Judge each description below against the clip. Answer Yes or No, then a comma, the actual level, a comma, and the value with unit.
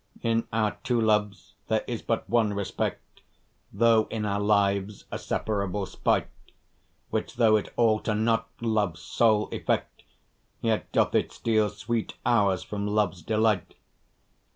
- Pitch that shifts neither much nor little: No, narrow, 1.8 semitones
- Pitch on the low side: Yes, low, 110 Hz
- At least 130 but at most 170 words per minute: Yes, slow, 135 wpm